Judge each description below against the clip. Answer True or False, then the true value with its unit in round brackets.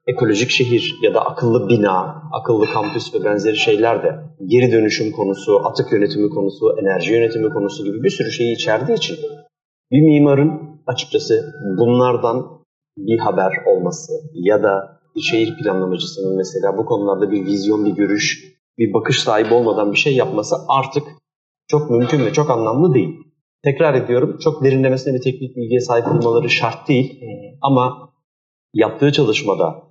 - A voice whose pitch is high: False (130 Hz)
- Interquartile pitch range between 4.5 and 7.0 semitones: True (5.1 semitones)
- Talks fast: True (150 wpm)